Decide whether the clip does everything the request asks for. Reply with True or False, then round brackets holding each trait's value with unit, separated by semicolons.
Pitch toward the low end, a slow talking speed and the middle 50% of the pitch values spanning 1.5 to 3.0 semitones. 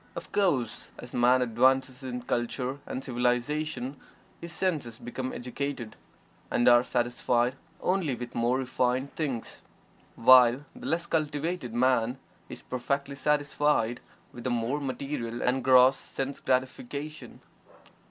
True (130 Hz; 125 wpm; 2.6 semitones)